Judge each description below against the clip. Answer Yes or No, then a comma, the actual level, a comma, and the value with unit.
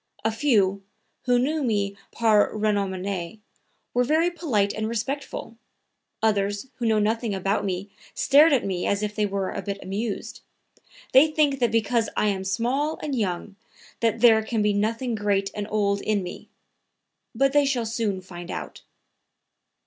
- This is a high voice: Yes, high, 215 Hz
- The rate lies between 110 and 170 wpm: Yes, average, 160 wpm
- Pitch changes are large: No, average, 3.5 semitones